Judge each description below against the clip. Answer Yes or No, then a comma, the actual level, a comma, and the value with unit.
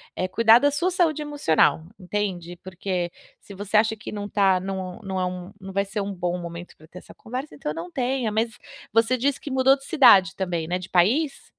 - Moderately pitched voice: No, high, 200 Hz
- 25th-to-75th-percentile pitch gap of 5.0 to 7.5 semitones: Yes, wide, 5.5 semitones